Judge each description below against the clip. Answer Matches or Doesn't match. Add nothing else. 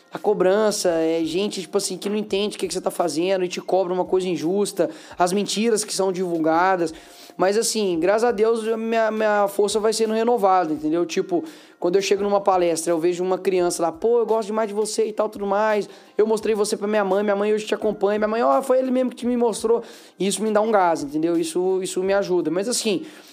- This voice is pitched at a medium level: Doesn't match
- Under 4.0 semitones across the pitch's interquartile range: Matches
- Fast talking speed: Matches